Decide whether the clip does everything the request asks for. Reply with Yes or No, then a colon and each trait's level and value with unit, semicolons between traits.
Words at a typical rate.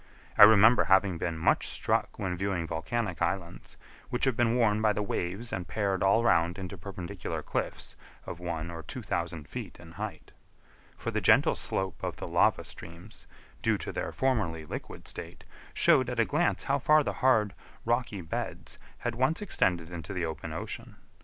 Yes: average, 180 wpm